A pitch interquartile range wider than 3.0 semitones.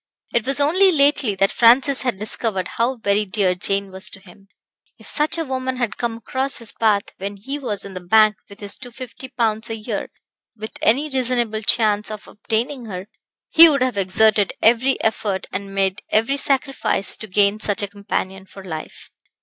Yes: average, 4.3 semitones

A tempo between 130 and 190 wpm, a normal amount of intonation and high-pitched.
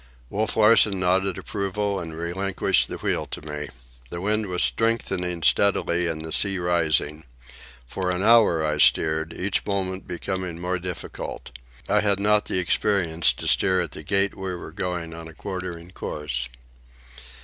No: average, 160 wpm; average, 3.0 semitones; very low, 90 Hz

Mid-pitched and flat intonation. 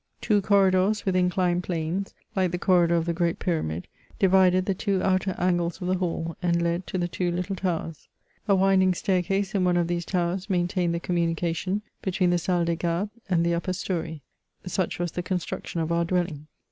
Yes: medium, 180 Hz; narrow, 1.7 semitones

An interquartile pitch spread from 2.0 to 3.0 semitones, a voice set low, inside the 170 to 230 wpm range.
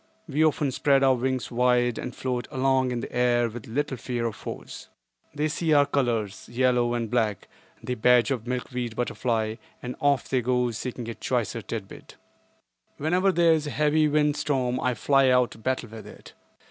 Yes: average, 2.7 semitones; low, 125 Hz; average, 180 wpm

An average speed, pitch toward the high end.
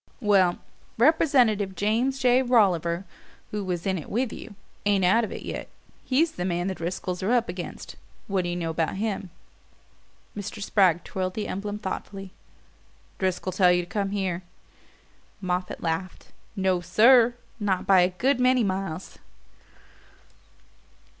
Yes: average, 145 wpm; high, 195 Hz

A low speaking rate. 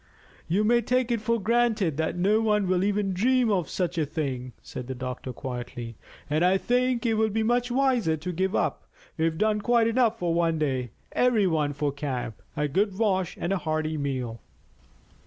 No: average, 195 wpm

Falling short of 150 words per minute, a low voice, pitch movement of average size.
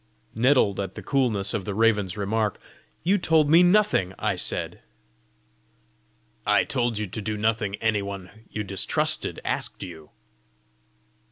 Yes: average, 140 wpm; low, 110 Hz; average, 3.8 semitones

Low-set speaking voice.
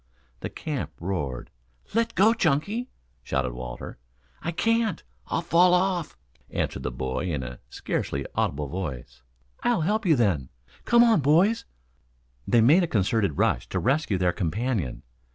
Yes: low, 120 Hz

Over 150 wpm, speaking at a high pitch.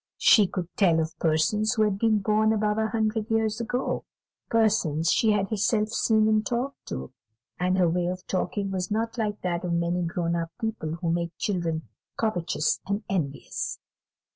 Yes: average, 175 wpm; high, 205 Hz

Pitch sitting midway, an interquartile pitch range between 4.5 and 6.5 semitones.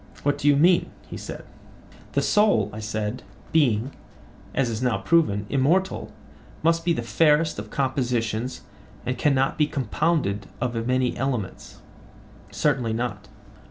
No: low, 130 Hz; average, 5.1 semitones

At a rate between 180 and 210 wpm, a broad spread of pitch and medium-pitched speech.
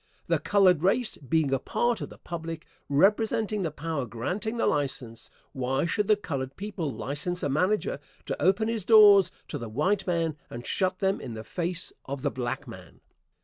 Yes: average, 185 wpm; wide, 6.7 semitones; medium, 165 Hz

